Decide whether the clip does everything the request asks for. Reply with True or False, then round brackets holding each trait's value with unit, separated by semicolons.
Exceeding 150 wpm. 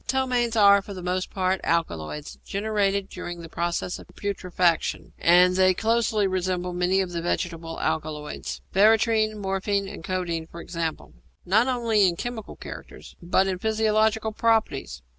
False (145 wpm)